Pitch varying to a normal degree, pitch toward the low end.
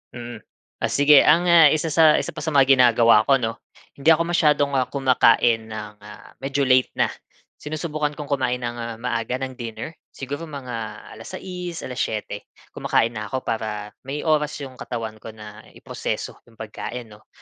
Yes: average, 4.4 semitones; low, 130 Hz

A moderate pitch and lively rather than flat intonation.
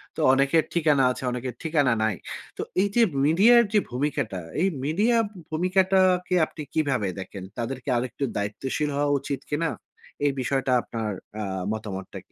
Yes: medium, 145 Hz; wide, 5.7 semitones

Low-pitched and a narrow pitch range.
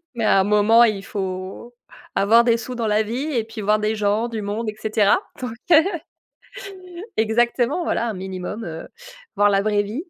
No: high, 215 Hz; narrow, 2.3 semitones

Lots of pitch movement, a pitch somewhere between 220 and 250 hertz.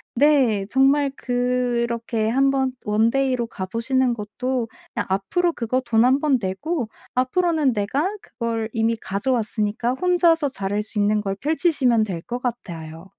No: average, 4.0 semitones; high, 240 Hz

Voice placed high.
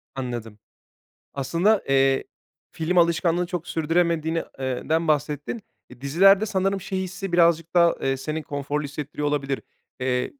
No: medium, 160 Hz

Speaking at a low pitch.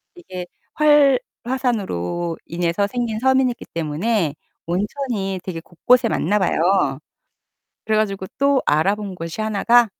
No: high, 205 Hz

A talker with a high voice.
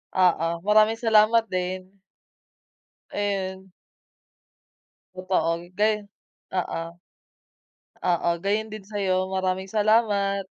Yes: high, 195 Hz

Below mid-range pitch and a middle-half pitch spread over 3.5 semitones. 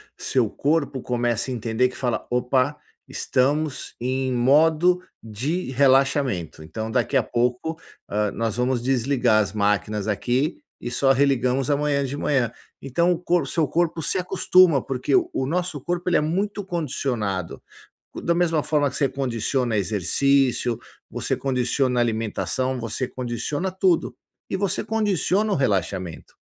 Yes: low, 130 Hz; average, 4.6 semitones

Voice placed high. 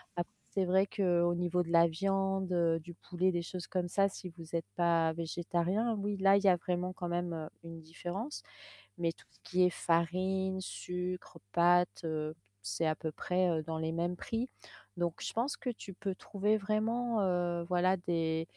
No: medium, 175 Hz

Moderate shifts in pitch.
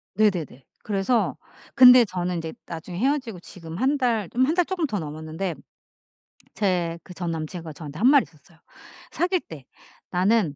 No: wide, 6.9 semitones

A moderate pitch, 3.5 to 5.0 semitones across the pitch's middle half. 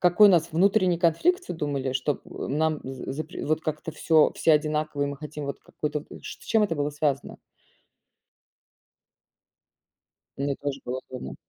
No: medium, 150 Hz; average, 2.7 semitones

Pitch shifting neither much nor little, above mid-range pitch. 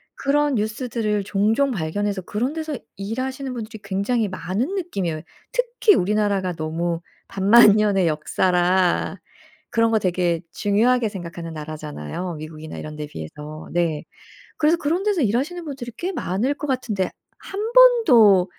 No: wide, 6.9 semitones; high, 205 Hz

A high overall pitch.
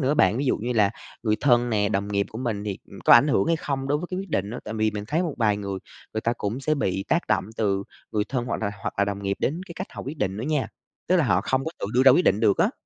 No: low, 115 Hz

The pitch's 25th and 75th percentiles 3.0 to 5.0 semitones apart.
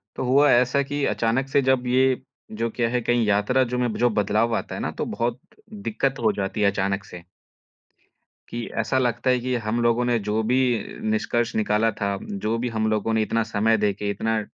No: narrow, 2.6 semitones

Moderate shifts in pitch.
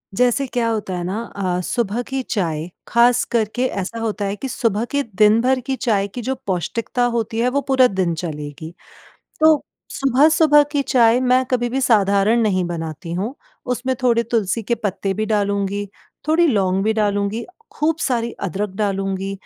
Yes: average, 4.2 semitones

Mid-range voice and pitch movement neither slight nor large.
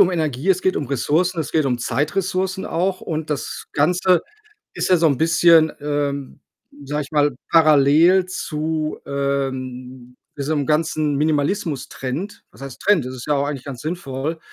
Yes: medium, 150 Hz; average, 3.3 semitones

